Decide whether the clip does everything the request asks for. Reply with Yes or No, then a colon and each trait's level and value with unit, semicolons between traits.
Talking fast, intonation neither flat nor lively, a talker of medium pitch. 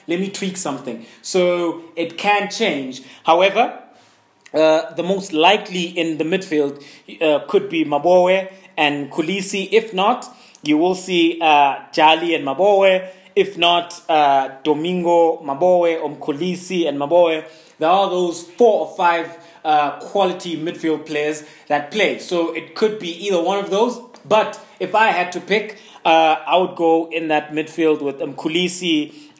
No: average, 150 wpm; average, 3.5 semitones; medium, 170 Hz